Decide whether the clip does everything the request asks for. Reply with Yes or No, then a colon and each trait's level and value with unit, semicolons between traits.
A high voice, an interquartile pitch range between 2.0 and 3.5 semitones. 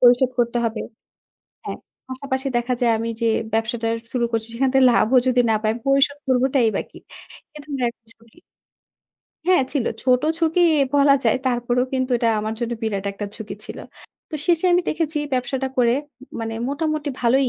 Yes: very high, 250 Hz; average, 3.0 semitones